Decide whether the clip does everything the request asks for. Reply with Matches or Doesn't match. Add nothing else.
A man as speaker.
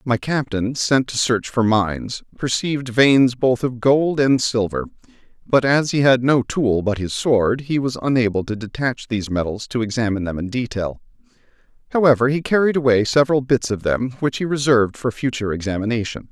Matches